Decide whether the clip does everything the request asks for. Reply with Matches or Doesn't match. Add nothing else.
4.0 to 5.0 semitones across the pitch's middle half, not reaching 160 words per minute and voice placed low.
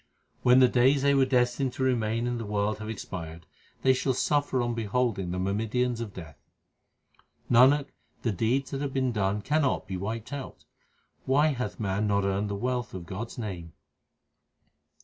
Doesn't match